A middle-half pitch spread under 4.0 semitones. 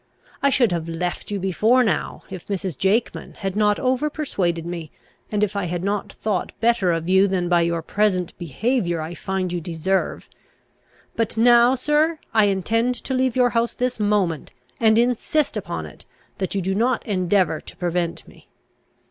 No: average, 5.0 semitones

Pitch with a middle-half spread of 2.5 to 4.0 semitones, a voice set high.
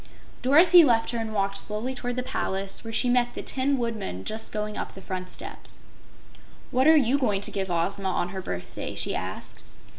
No: average, 4.5 semitones; high, 220 Hz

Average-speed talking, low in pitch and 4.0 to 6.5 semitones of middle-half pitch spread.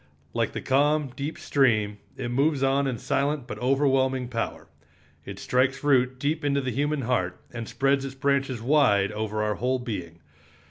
No: average, 170 wpm; low, 130 Hz; average, 3.0 semitones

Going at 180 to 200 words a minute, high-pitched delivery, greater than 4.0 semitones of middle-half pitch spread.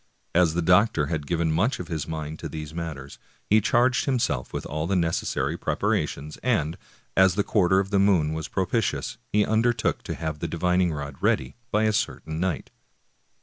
No: average, 190 wpm; very low, 85 Hz; average, 4.4 semitones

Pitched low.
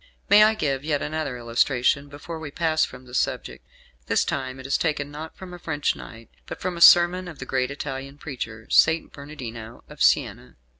No: medium, 145 Hz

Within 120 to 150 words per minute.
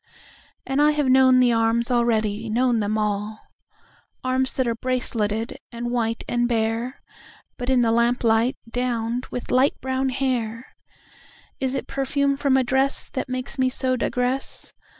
Yes: slow, 135 wpm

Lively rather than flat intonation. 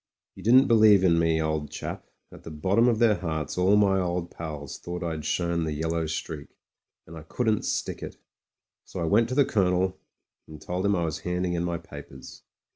No: average, 3.7 semitones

